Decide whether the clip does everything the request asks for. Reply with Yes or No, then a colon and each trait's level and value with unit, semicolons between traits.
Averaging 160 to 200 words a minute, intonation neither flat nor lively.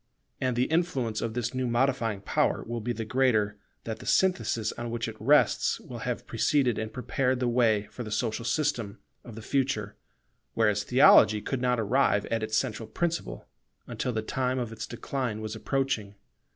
Yes: average, 180 wpm; average, 3.0 semitones